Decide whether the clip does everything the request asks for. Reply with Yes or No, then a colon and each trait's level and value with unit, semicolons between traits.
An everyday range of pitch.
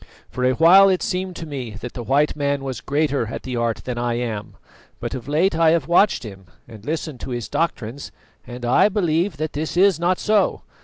No: wide, 5.7 semitones